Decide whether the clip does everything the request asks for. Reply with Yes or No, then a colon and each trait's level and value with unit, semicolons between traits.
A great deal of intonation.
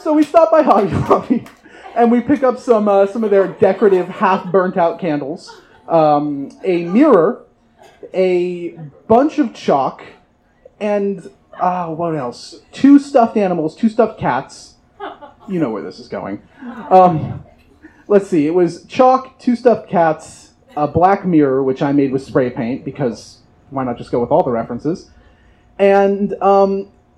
Yes: wide, 6.5 semitones